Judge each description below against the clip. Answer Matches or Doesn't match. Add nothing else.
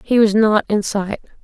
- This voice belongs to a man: Doesn't match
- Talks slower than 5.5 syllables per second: Matches